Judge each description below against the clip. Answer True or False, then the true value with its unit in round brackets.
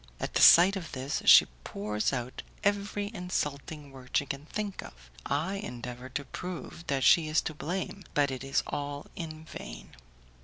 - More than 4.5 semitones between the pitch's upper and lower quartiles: True (5.3 semitones)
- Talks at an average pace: True (175 wpm)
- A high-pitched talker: False (145 Hz)